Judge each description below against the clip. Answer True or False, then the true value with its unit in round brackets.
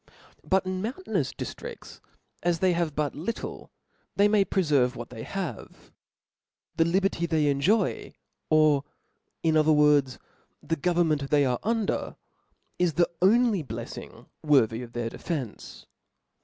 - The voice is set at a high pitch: False (160 Hz)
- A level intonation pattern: False (5.0 semitones)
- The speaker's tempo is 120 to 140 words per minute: True (135 wpm)